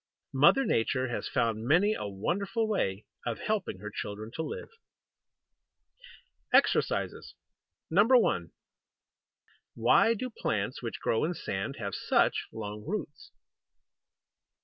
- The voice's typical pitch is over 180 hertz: No, low, 130 Hz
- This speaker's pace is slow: Yes, slow, 110 wpm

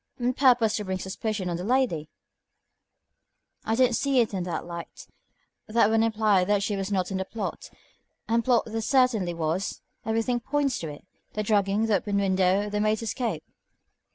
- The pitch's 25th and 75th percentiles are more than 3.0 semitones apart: Yes, average, 3.4 semitones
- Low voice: No, high, 210 Hz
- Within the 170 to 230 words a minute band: Yes, average, 180 wpm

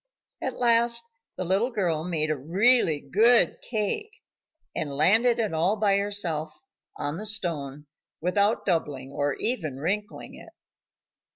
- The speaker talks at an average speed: No, slow, 130 wpm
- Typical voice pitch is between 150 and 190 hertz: Yes, medium, 185 Hz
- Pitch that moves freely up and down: Yes, wide, 6.0 semitones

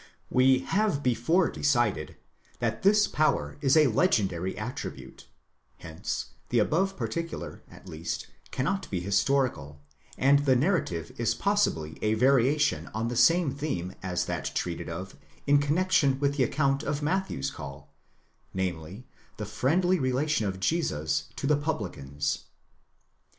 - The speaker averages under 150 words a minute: Yes, slow, 135 wpm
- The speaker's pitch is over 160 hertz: No, low, 130 Hz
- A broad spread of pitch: Yes, wide, 8.1 semitones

